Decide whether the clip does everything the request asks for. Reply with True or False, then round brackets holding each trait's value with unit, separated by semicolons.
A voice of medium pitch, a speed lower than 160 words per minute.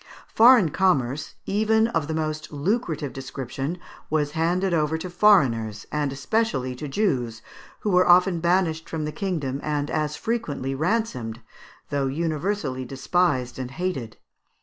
True (155 Hz; 135 wpm)